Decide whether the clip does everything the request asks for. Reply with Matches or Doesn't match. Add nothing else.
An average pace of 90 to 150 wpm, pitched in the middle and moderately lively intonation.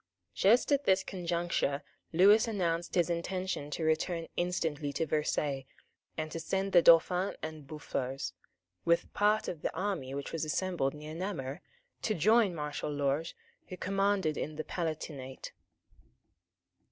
Matches